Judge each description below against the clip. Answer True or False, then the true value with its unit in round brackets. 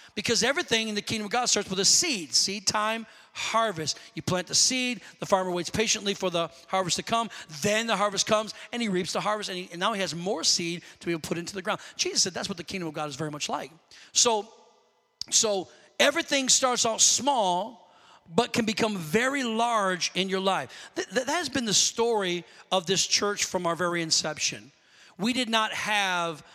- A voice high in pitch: True (205 Hz)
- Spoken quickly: True (215 wpm)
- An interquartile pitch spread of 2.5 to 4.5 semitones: True (4.2 semitones)